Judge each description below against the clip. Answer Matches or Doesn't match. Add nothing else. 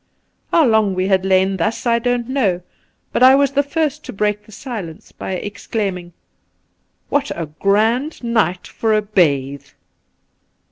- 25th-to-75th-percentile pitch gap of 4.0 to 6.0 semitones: Matches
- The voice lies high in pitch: Matches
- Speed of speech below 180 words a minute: Matches